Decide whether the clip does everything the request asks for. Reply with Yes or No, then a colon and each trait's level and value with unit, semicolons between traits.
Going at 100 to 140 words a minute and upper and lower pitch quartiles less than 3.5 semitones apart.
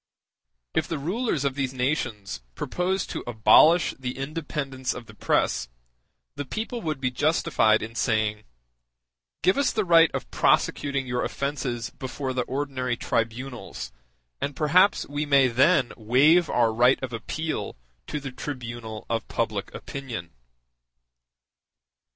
No: slow, 135 wpm; average, 4.2 semitones